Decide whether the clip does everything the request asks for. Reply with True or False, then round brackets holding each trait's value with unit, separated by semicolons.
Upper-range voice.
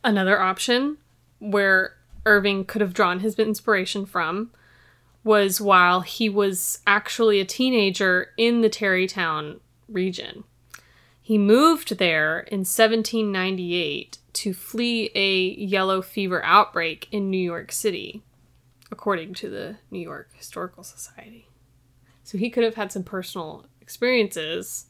True (195 Hz)